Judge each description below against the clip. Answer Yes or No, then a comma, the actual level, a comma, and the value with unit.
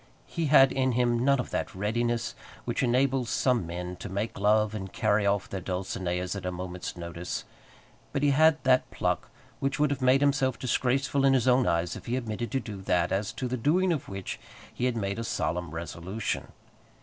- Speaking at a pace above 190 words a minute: Yes, average, 200 wpm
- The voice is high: No, low, 115 Hz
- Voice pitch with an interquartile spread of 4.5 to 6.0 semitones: Yes, wide, 5.5 semitones